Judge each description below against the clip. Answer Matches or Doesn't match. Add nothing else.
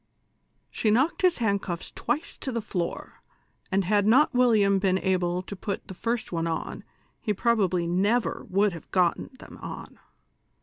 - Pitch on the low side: Doesn't match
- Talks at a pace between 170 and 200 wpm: Doesn't match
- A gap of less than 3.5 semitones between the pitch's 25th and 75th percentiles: Doesn't match